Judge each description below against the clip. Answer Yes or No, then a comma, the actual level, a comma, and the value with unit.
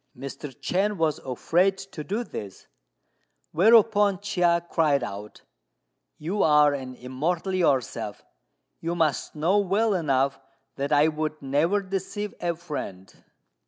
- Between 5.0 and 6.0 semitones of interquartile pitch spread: Yes, wide, 5.4 semitones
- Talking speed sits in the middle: No, slow, 125 wpm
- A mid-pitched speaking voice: Yes, medium, 165 Hz